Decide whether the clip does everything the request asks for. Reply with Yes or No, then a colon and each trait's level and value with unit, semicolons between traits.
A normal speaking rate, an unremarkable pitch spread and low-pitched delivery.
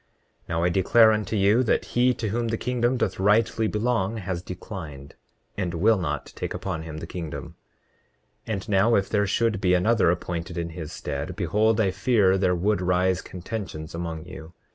Yes: average, 185 wpm; average, 4.2 semitones; very low, 95 Hz